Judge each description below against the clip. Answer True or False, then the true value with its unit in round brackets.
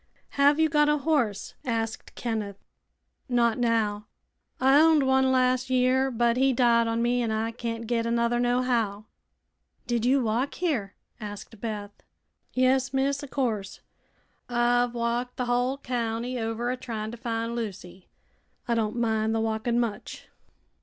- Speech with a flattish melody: True (2.3 semitones)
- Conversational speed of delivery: True (150 wpm)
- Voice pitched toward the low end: False (240 Hz)